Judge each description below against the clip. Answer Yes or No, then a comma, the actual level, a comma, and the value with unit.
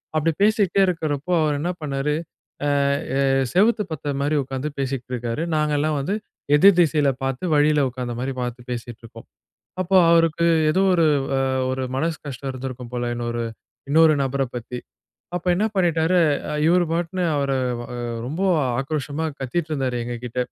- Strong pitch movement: No, average, 4.3 semitones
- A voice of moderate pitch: Yes, medium, 145 Hz